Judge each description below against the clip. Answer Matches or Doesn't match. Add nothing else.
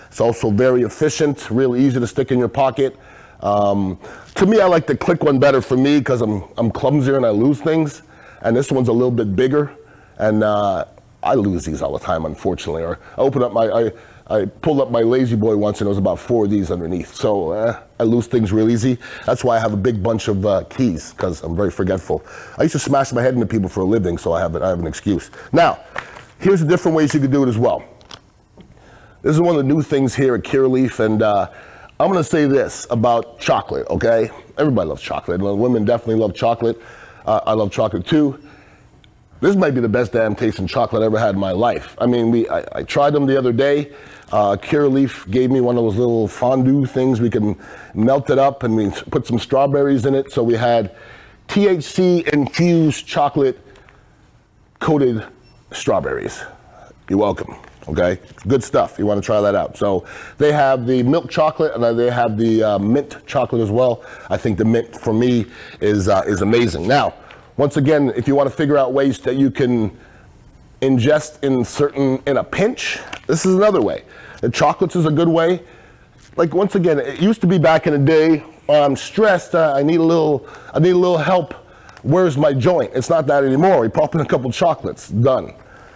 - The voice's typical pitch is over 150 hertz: Doesn't match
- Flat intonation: Doesn't match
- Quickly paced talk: Matches